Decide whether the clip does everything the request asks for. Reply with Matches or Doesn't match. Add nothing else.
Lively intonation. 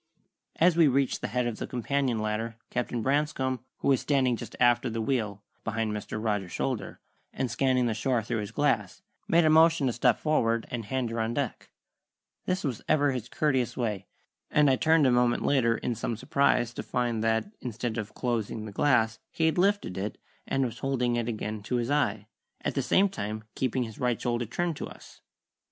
Doesn't match